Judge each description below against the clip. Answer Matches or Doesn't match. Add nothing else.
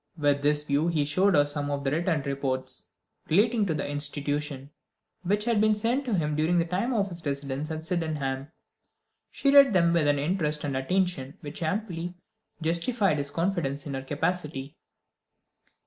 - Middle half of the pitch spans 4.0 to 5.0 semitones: Matches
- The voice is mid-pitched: Matches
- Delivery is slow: Doesn't match